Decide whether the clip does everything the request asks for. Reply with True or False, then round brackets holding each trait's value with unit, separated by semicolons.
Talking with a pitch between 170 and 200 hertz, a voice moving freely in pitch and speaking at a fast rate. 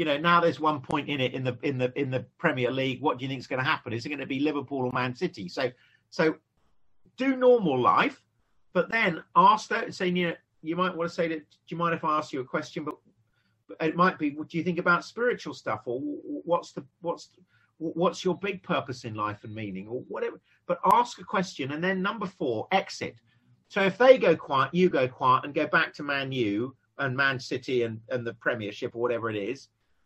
False (155 Hz; 6.0 semitones; 240 wpm)